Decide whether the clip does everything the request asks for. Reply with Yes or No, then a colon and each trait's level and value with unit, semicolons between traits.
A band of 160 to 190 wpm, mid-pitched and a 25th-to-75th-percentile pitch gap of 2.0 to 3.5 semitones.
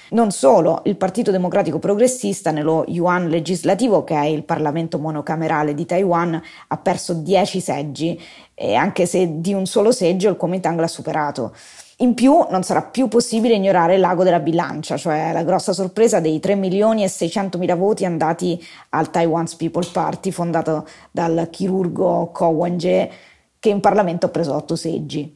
Yes: average, 165 wpm; medium, 175 Hz; average, 2.8 semitones